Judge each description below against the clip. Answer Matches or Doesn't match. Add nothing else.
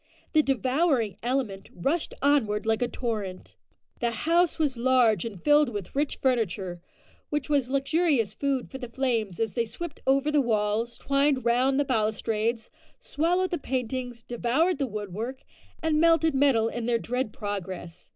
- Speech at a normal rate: Matches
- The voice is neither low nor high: Doesn't match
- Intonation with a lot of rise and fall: Doesn't match